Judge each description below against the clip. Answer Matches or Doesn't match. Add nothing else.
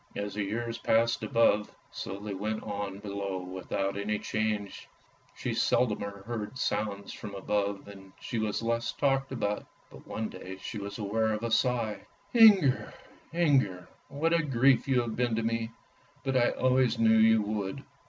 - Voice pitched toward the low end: Matches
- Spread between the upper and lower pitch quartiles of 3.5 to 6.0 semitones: Doesn't match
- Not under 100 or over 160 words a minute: Doesn't match